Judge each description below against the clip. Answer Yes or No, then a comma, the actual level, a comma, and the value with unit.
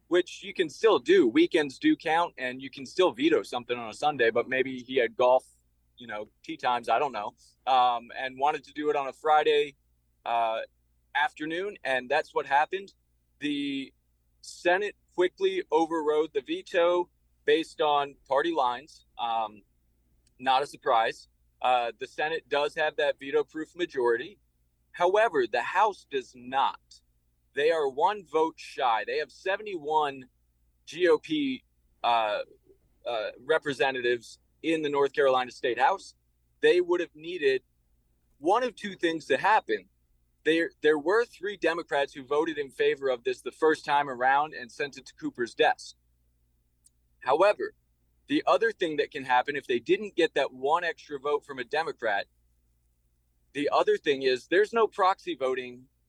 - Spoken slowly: No, average, 155 wpm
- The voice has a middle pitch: Yes, medium, 145 Hz